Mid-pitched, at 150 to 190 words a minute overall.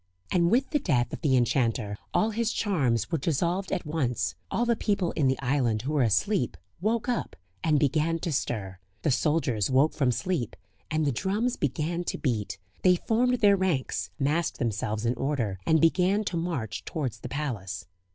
Yes: medium, 150 Hz; average, 180 wpm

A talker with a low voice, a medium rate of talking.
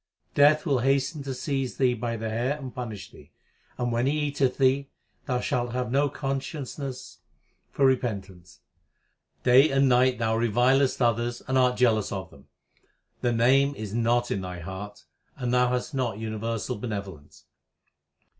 Yes: low, 125 Hz; average, 160 wpm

